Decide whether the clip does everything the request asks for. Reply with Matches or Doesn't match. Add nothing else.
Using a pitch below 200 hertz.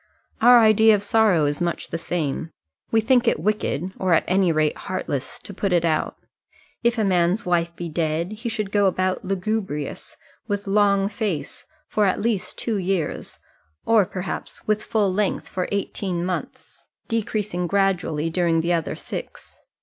Matches